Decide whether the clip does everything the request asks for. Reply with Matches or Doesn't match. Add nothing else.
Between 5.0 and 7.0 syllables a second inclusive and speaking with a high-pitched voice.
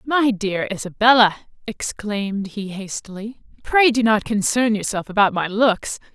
Doesn't match